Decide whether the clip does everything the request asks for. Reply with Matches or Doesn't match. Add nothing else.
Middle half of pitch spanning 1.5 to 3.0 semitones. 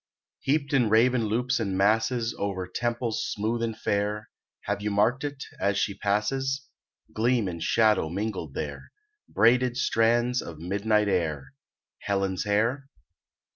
Doesn't match